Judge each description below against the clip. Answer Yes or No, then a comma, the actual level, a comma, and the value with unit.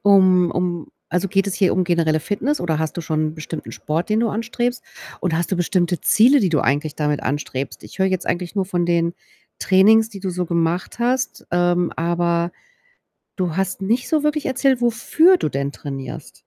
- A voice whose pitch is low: No, medium, 180 Hz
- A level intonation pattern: No, average, 4.3 semitones